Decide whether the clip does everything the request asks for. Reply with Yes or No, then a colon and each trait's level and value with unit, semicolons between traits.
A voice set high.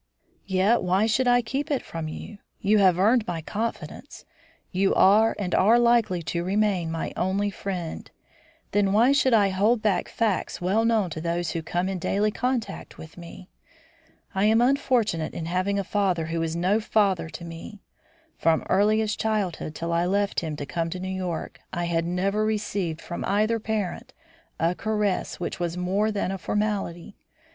Yes: high, 195 Hz